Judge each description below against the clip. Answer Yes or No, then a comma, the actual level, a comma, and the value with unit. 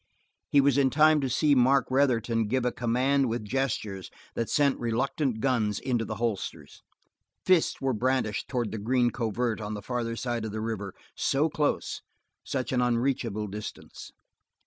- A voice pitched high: No, low, 120 Hz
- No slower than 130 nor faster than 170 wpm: Yes, average, 165 wpm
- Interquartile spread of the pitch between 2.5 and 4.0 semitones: Yes, average, 3.4 semitones